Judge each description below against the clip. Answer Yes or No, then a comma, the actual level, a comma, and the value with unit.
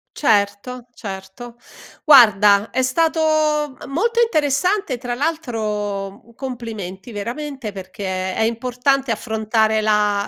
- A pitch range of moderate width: Yes, average, 4.6 semitones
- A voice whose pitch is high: Yes, high, 230 Hz